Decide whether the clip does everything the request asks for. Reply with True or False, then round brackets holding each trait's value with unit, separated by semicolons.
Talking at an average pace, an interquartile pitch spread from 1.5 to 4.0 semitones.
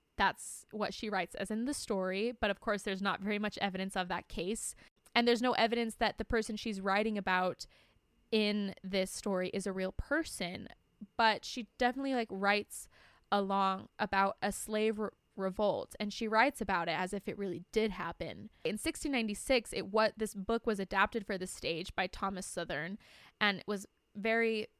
True (185 wpm; 2.5 semitones)